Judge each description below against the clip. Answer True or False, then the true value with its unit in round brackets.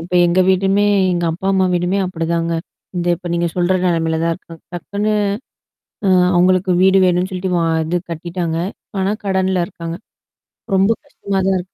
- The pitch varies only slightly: True (1.9 semitones)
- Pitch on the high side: False (180 Hz)